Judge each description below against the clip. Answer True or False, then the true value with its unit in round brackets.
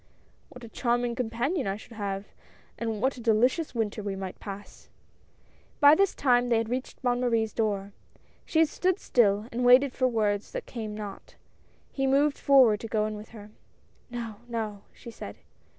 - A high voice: True (230 Hz)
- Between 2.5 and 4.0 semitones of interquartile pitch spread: True (3.0 semitones)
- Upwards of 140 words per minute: True (180 wpm)